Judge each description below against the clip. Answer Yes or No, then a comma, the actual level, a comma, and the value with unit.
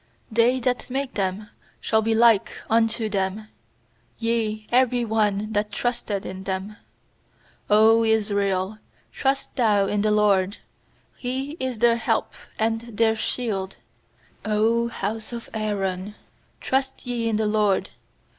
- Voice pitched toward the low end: No, high, 220 Hz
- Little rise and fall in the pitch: Yes, narrow, 2.3 semitones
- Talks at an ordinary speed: No, slow, 125 wpm